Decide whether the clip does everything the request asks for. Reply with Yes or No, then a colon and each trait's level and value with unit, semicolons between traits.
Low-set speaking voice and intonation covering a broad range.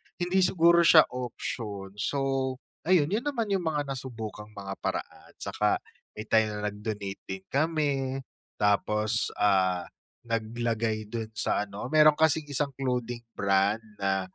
Yes: low, 115 Hz; wide, 6.1 semitones